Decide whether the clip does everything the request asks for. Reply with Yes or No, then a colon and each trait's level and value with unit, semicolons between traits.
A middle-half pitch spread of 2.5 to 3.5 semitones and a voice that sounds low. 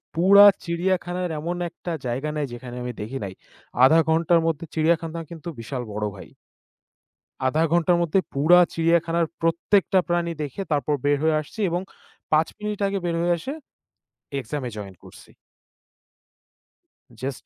No: average, 3.2 semitones; medium, 165 Hz